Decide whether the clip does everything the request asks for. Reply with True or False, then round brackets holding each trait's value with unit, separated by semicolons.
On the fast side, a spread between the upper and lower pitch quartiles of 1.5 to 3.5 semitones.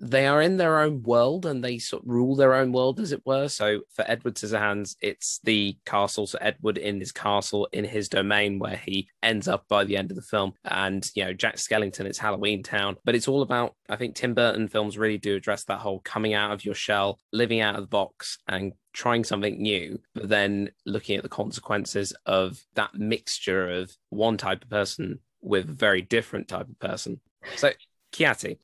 True (210 wpm; 3.1 semitones)